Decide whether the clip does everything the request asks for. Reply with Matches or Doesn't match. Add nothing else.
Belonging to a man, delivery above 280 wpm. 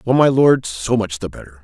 Doesn't match